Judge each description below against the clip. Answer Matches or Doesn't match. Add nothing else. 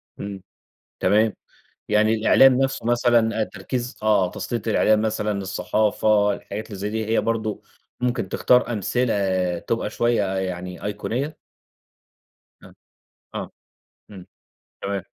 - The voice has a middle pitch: Doesn't match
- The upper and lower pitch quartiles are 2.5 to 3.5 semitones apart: Matches